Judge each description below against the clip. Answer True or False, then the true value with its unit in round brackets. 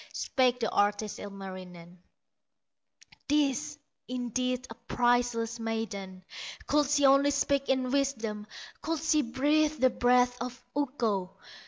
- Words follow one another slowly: True (115 wpm)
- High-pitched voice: True (245 Hz)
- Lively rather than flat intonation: False (3.9 semitones)